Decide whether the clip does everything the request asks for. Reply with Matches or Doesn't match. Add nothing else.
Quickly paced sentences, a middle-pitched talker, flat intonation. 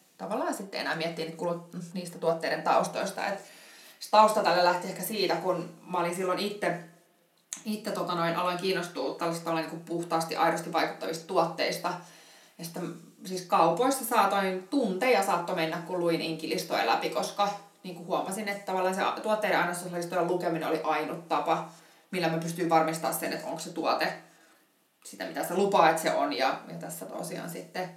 Matches